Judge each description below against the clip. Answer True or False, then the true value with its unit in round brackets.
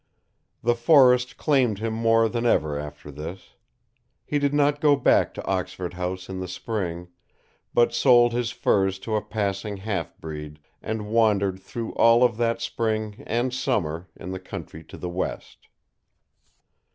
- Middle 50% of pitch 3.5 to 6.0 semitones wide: True (4.4 semitones)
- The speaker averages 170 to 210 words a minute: False (155 wpm)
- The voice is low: True (110 Hz)